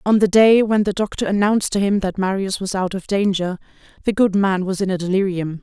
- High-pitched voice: Yes, high, 195 Hz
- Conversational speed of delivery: No, fast, 235 wpm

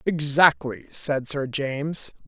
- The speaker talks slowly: Yes, slow, 105 wpm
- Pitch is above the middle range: No, medium, 145 Hz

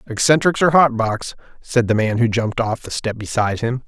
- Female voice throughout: No, male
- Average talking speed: No, fast, 215 wpm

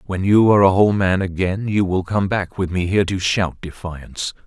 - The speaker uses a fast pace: Yes, fast, 230 wpm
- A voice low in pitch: Yes, very low, 95 Hz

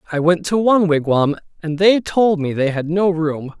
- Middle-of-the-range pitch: Yes, medium, 170 Hz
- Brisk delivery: Yes, fast, 215 wpm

